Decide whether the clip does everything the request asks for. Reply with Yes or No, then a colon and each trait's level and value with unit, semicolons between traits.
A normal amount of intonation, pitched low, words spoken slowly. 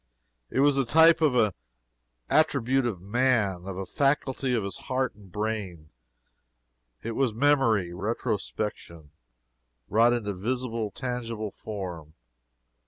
Yes: average, 4.8 semitones; low, 115 Hz; slow, 120 wpm